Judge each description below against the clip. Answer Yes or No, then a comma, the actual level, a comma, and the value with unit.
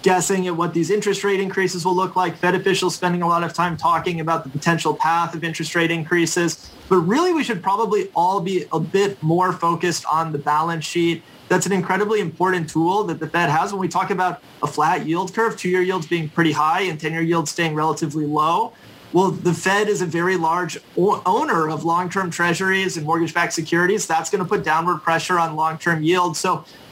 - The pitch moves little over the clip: Yes, narrow, 2.3 semitones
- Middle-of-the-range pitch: Yes, medium, 175 Hz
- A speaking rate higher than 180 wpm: Yes, fast, 205 wpm